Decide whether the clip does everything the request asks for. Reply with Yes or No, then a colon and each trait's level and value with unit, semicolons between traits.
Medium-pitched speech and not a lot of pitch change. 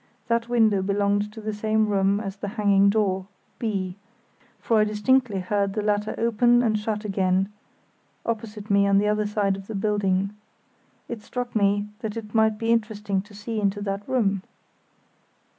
No: high, 210 Hz; narrow, 1.7 semitones